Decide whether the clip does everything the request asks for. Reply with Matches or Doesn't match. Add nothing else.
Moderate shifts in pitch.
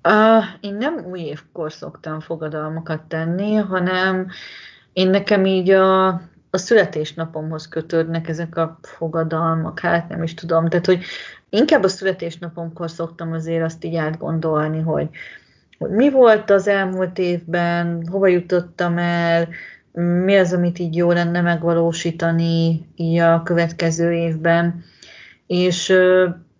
Doesn't match